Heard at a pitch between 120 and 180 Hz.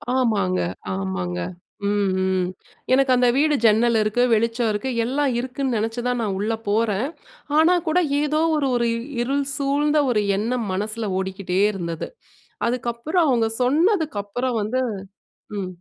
No: high, 235 Hz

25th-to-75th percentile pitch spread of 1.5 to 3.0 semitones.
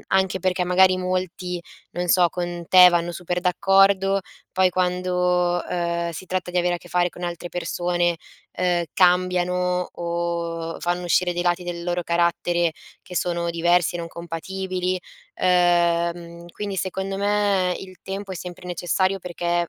No: narrow, 1.0 semitones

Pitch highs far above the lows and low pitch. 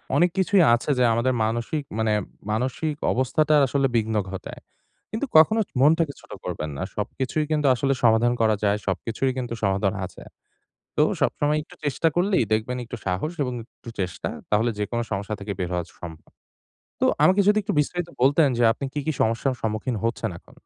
Yes: wide, 5.8 semitones; low, 125 Hz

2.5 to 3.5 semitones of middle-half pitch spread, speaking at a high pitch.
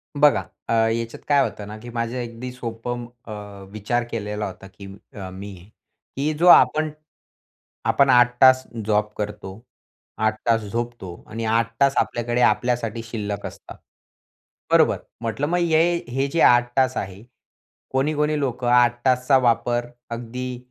No: average, 3.0 semitones; low, 120 Hz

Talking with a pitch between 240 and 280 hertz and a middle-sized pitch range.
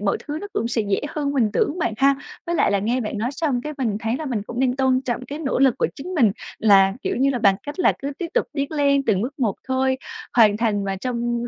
Yes: very high, 250 Hz; average, 4.3 semitones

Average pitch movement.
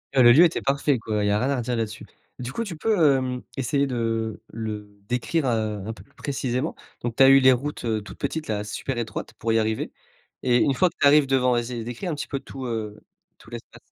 Yes: average, 3.6 semitones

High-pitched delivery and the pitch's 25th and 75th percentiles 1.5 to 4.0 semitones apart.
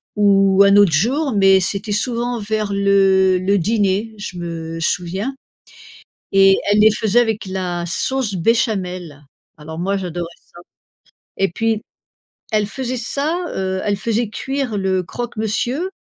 Yes: high, 200 Hz; average, 3.2 semitones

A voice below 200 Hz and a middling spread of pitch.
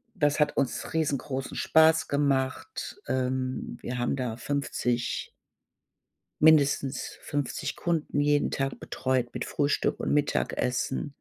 No: medium, 140 Hz; narrow, 2.2 semitones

